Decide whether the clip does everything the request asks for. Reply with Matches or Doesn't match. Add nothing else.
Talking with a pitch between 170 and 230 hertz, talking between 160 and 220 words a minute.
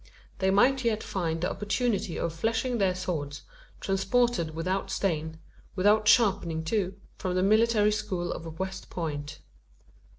Doesn't match